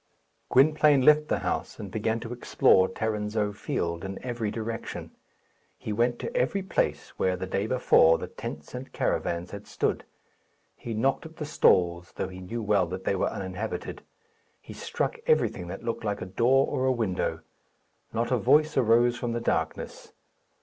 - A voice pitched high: No, low, 110 Hz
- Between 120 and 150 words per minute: No, average, 170 wpm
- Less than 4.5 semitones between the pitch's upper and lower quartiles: No, average, 5.0 semitones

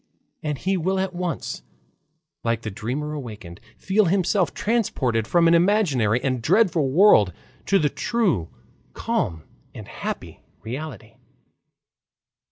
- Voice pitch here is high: No, medium, 150 Hz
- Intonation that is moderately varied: No, wide, 8.5 semitones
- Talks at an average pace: No, slow, 120 wpm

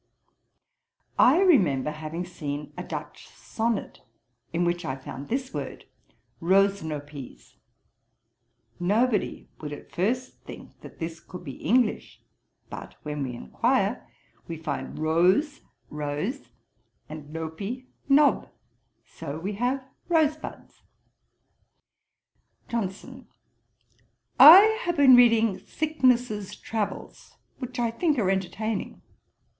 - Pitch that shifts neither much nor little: No, wide, 8.2 semitones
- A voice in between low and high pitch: No, high, 195 Hz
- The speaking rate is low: Yes, slow, 105 wpm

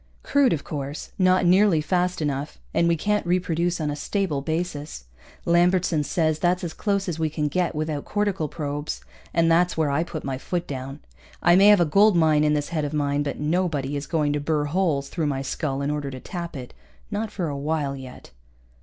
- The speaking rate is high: Yes, fast, 215 wpm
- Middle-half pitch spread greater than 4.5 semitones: No, average, 3.5 semitones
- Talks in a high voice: No, medium, 155 Hz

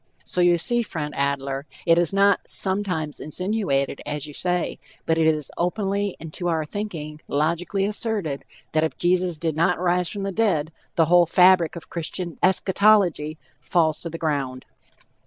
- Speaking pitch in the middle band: Yes, medium, 170 Hz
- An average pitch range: Yes, average, 3.5 semitones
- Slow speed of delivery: No, average, 165 wpm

